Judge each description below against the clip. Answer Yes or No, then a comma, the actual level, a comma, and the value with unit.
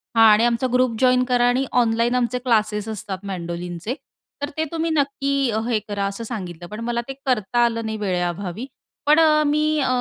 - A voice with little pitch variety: No, average, 4.2 semitones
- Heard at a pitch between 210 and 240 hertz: Yes, high, 235 Hz